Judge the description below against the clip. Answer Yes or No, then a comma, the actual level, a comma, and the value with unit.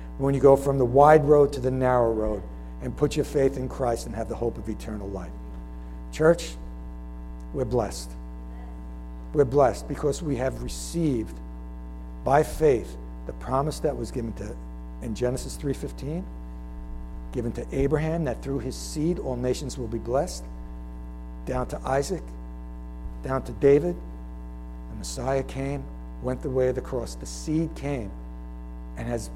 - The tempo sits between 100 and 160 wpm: Yes, average, 155 wpm